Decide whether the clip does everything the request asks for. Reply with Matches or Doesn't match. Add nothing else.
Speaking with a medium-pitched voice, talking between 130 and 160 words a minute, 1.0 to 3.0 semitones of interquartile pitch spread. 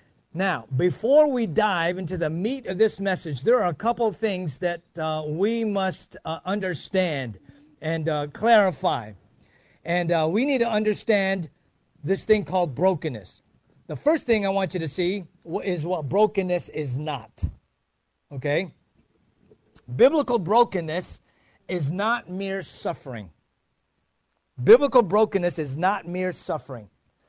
Doesn't match